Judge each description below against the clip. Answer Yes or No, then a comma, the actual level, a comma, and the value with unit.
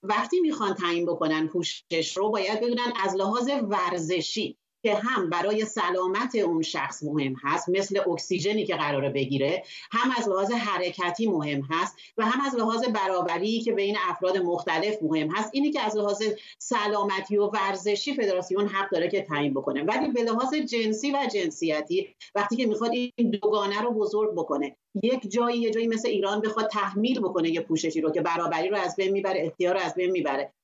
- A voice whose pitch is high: Yes, high, 205 Hz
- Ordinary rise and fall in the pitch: Yes, average, 4.5 semitones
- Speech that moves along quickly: Yes, fast, 180 wpm